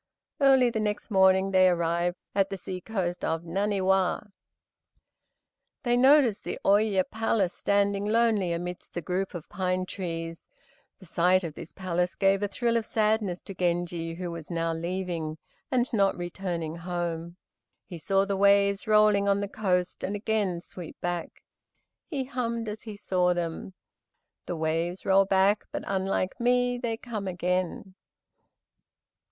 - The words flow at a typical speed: Yes, average, 150 wpm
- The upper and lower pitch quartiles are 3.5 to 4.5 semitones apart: No, average, 3.1 semitones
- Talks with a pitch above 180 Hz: Yes, high, 190 Hz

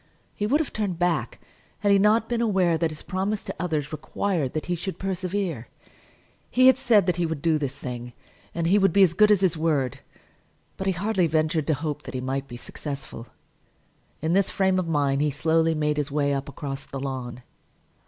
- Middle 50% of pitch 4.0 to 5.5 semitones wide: Yes, average, 5.2 semitones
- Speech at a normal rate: No, fast, 210 wpm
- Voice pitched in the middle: Yes, medium, 165 Hz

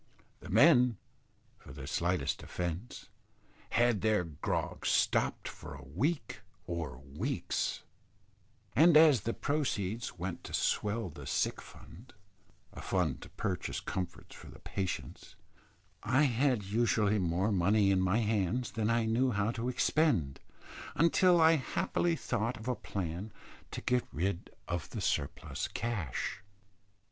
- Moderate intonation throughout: No, wide, 5.7 semitones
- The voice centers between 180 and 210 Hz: No, low, 105 Hz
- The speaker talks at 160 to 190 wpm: No, slow, 135 wpm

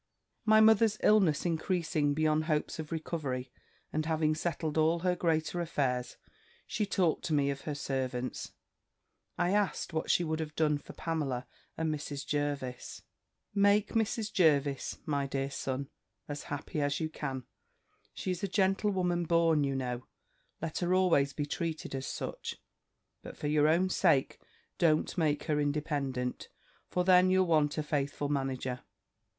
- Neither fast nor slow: Yes, average, 155 wpm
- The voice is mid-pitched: Yes, medium, 155 Hz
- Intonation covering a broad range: No, average, 3.6 semitones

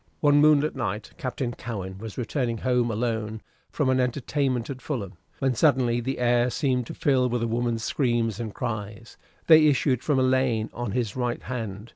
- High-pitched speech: No, low, 120 Hz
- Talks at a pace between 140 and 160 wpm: No, average, 180 wpm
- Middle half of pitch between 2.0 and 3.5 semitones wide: Yes, narrow, 2.5 semitones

